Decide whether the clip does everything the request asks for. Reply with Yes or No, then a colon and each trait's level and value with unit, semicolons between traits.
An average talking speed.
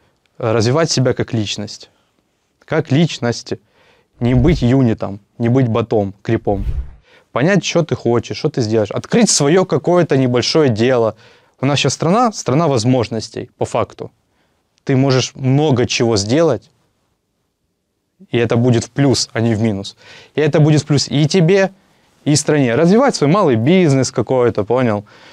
Yes: average, 145 wpm